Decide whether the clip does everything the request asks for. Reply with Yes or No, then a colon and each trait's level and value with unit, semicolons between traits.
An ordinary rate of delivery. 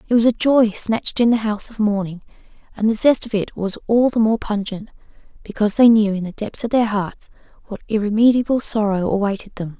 No: fast, 210 wpm